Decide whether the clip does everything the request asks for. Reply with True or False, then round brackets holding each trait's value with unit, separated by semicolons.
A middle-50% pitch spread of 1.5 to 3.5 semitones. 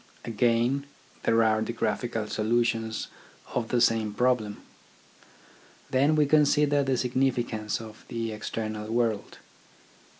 True (2.6 semitones)